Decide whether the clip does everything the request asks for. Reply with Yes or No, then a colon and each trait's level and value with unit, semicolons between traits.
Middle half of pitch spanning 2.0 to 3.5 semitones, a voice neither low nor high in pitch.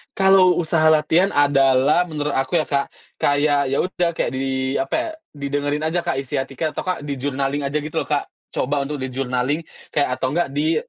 Yes: average, 2.8 semitones; medium, 145 Hz